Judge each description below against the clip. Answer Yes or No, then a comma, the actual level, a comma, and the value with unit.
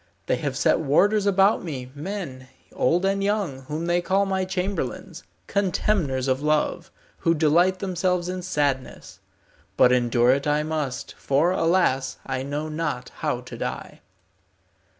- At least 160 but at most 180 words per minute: No, average, 145 wpm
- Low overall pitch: No, medium, 160 Hz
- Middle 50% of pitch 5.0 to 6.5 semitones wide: Yes, wide, 5.5 semitones